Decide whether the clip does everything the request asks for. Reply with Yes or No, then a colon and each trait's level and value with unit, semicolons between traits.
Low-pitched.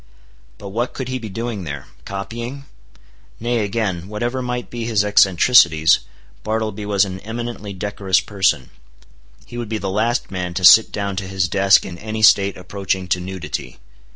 Yes: low, 100 Hz